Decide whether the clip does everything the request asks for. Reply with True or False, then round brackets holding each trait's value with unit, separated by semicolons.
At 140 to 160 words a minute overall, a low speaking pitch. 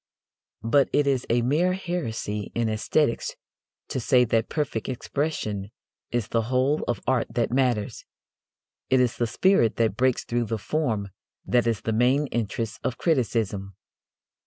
True (150 wpm; 120 Hz)